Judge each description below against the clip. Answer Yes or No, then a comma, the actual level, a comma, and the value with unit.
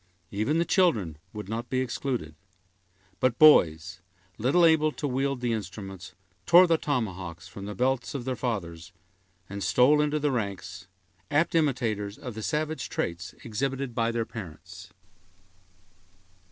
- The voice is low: Yes, low, 115 Hz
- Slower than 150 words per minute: Yes, average, 140 wpm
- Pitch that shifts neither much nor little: No, wide, 6.3 semitones